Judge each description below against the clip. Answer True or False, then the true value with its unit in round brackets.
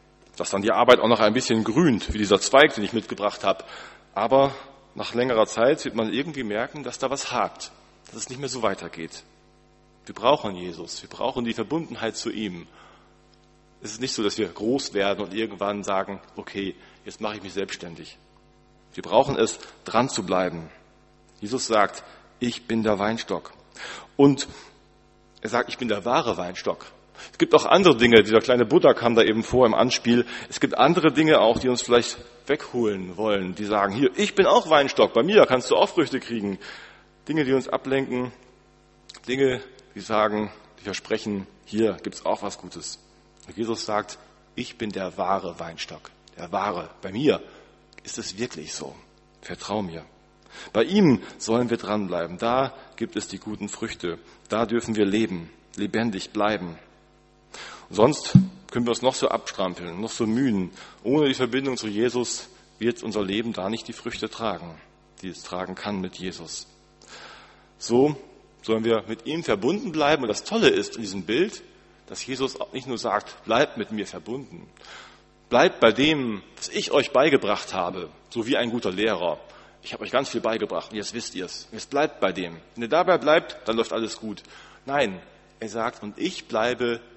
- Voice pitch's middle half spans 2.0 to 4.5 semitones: True (3.6 semitones)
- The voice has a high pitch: False (115 Hz)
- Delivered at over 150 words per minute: True (180 wpm)